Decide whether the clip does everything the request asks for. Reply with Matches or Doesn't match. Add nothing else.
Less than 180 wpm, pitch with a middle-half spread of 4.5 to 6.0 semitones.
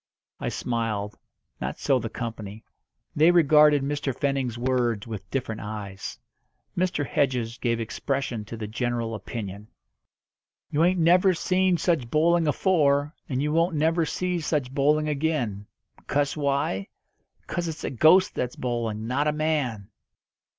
Matches